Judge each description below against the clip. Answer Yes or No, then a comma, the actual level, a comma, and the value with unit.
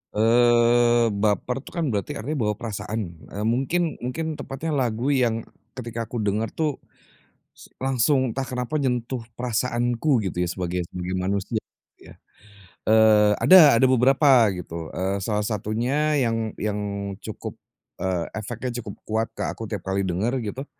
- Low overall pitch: Yes, low, 115 Hz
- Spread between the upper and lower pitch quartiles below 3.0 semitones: No, average, 3.5 semitones